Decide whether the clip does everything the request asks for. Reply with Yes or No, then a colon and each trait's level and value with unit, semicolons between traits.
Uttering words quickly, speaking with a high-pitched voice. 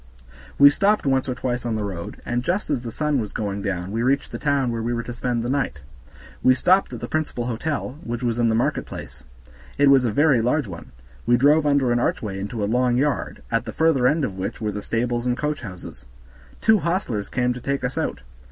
No: fast, 235 wpm; low, 125 Hz